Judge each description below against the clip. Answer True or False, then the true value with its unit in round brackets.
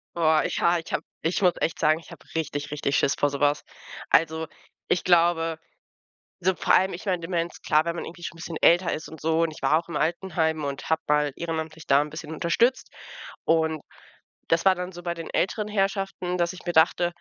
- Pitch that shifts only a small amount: True (1.8 semitones)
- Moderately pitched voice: True (165 Hz)